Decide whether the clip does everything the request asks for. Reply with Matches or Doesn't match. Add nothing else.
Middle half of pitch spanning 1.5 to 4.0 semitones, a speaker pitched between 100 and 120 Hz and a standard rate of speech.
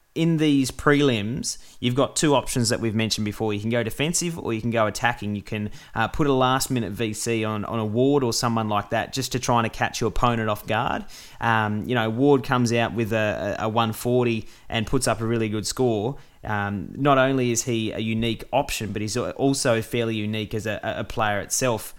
Doesn't match